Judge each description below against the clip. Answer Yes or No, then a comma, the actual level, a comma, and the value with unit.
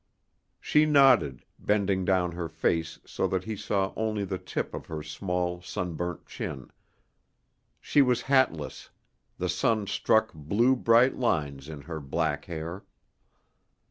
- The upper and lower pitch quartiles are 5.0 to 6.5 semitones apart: Yes, wide, 5.4 semitones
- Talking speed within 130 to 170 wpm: Yes, slow, 135 wpm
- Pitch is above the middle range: No, very low, 90 Hz